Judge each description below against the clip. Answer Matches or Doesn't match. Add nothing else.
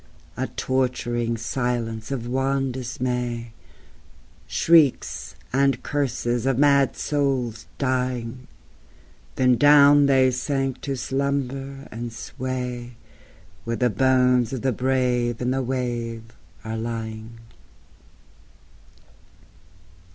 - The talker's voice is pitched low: Matches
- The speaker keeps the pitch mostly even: Matches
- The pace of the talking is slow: Matches